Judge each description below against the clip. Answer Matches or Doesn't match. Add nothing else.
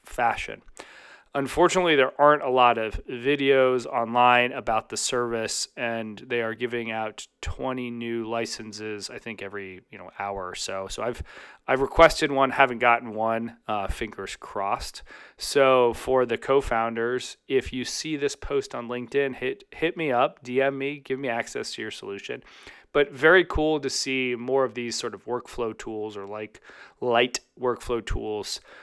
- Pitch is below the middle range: Matches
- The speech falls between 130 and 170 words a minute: Matches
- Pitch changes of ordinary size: Matches